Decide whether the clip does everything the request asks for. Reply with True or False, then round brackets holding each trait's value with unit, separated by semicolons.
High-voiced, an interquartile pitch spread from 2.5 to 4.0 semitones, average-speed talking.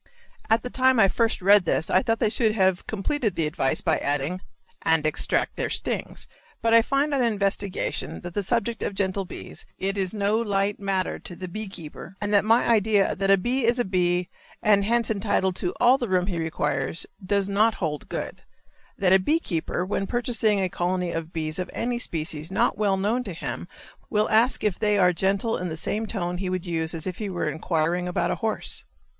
False (195 Hz; 3.7 semitones; 210 wpm)